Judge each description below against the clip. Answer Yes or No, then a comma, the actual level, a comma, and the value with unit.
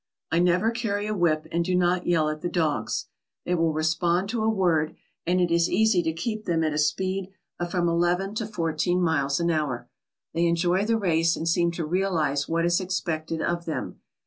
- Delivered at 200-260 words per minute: Yes, fast, 205 wpm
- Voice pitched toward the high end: No, medium, 175 Hz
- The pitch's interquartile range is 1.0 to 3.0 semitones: Yes, narrow, 2.4 semitones